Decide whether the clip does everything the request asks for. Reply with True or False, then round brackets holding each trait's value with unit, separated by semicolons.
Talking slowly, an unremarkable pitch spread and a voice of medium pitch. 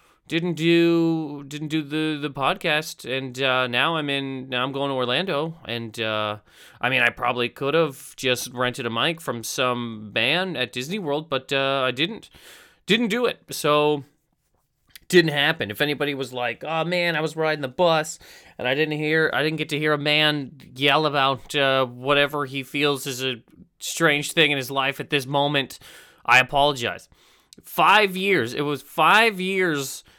False (180 wpm; 3.3 semitones; 145 Hz)